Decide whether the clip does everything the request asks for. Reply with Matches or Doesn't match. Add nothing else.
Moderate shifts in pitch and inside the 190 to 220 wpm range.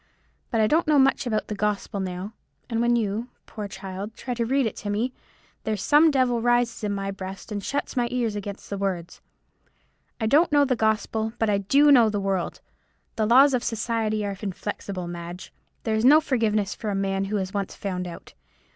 Matches